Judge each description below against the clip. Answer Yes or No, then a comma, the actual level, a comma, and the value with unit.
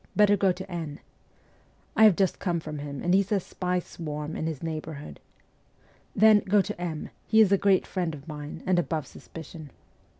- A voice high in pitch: No, medium, 175 Hz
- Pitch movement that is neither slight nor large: Yes, average, 3.9 semitones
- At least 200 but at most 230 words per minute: Yes, fast, 205 wpm